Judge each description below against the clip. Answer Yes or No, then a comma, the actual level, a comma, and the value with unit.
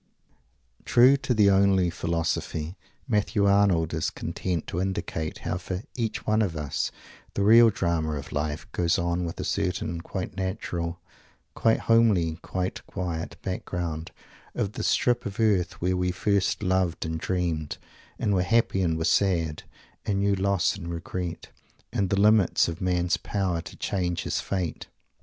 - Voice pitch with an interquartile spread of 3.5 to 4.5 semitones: No, average, 3.0 semitones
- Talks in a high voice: No, very low, 90 Hz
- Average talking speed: Yes, average, 155 wpm